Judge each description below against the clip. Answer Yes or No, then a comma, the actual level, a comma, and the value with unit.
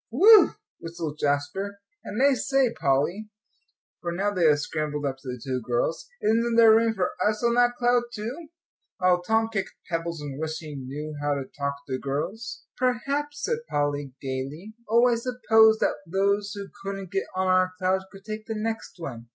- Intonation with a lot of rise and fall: Yes, wide, 7.3 semitones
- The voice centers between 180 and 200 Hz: Yes, high, 190 Hz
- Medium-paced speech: Yes, average, 185 wpm